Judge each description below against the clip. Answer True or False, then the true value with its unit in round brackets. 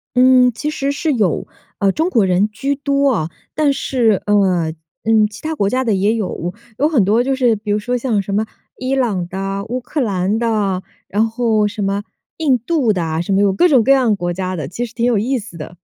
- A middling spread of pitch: True (4.6 semitones)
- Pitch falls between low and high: False (220 Hz)